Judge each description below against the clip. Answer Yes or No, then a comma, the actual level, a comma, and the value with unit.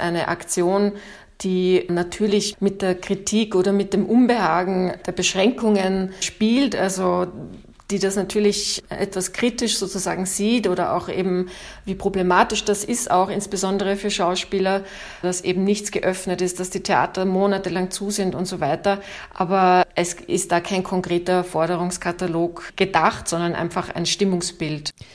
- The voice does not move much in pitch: Yes, narrow, 1.8 semitones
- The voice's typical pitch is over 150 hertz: Yes, medium, 185 Hz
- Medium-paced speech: Yes, average, 140 wpm